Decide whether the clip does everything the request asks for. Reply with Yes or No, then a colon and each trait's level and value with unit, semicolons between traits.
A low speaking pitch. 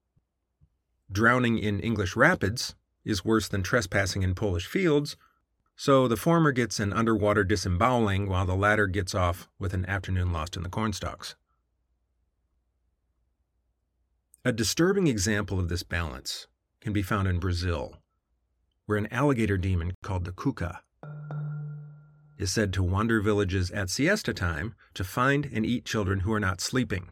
Yes: low, 100 Hz